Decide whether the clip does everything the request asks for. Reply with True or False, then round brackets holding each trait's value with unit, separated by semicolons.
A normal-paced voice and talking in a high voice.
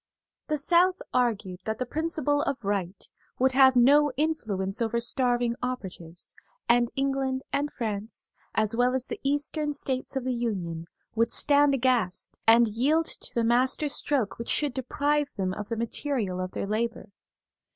True (160 wpm; 245 Hz)